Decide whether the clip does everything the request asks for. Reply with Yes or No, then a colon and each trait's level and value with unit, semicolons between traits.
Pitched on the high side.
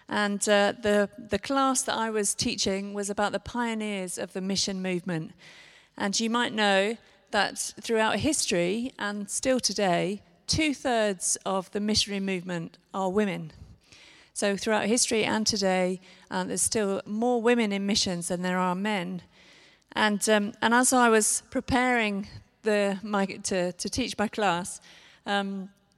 Yes: high, 205 Hz